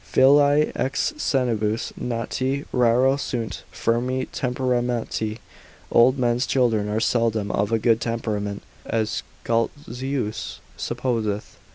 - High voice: No, low, 120 Hz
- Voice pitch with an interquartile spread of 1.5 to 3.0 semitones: Yes, average, 2.7 semitones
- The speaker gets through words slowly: Yes, slow, 105 wpm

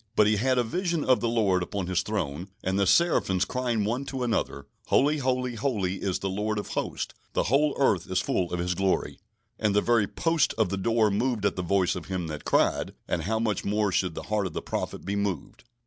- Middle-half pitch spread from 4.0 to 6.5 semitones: Yes, average, 4.3 semitones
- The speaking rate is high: Yes, fast, 230 wpm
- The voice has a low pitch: Yes, low, 105 Hz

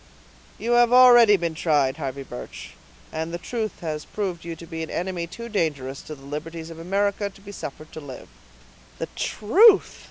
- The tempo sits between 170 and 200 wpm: Yes, average, 185 wpm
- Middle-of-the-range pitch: Yes, medium, 170 Hz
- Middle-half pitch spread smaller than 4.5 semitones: No, average, 5.0 semitones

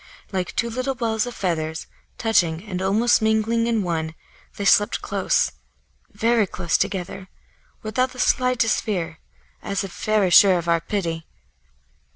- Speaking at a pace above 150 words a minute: No, average, 145 wpm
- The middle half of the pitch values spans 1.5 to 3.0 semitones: No, average, 4.6 semitones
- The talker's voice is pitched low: No, high, 205 Hz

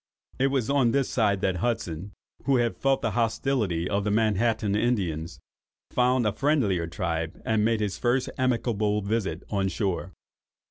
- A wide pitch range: No, average, 4.2 semitones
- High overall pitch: No, low, 110 Hz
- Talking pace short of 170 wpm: Yes, average, 155 wpm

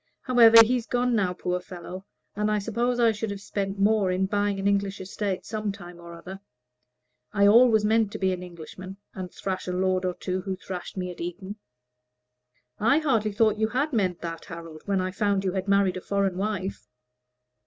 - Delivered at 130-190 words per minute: No, average, 200 wpm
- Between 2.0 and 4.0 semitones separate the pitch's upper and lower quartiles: Yes, average, 2.7 semitones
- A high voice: Yes, high, 195 Hz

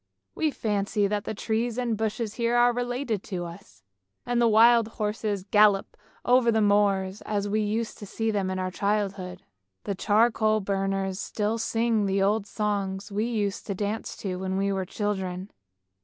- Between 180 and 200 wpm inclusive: No, average, 170 wpm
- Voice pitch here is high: Yes, high, 210 Hz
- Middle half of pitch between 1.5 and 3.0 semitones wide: Yes, narrow, 2.4 semitones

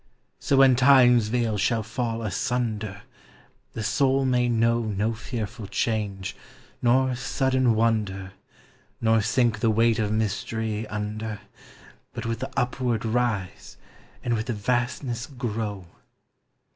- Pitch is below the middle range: Yes, low, 115 Hz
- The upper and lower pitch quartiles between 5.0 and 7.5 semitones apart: No, narrow, 2.4 semitones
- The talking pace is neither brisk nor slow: No, slow, 120 wpm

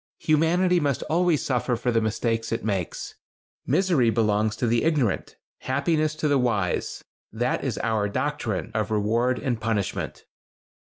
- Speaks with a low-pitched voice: Yes, low, 120 Hz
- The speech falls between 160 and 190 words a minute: No, average, 145 wpm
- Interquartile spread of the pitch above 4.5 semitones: Yes, average, 5.2 semitones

